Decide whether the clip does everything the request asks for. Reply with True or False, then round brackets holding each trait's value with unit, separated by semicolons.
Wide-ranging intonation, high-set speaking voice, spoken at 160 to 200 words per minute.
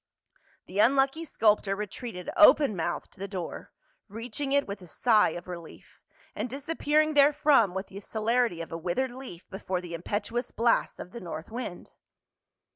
True (6.5 semitones; 215 Hz; 165 wpm)